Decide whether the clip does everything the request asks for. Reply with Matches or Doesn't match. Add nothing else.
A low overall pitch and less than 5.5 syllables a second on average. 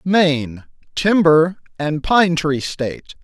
Doesn't match